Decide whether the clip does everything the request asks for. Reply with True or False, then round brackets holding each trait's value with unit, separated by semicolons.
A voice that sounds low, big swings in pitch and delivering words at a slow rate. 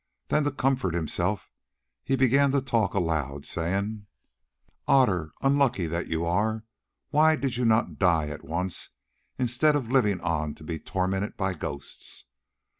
False (100 Hz; 7.5 semitones; 145 wpm)